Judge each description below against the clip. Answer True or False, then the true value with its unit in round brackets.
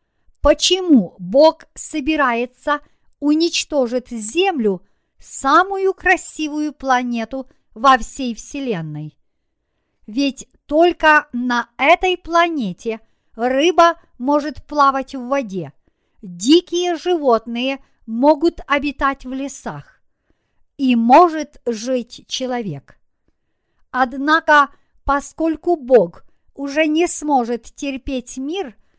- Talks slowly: True (80 wpm)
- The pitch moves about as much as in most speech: True (4.2 semitones)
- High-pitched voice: True (275 Hz)